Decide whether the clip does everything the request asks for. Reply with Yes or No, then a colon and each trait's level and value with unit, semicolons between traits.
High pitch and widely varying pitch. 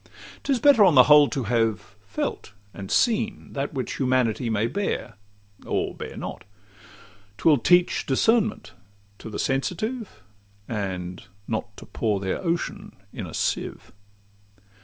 No: low, 130 Hz; wide, 9.0 semitones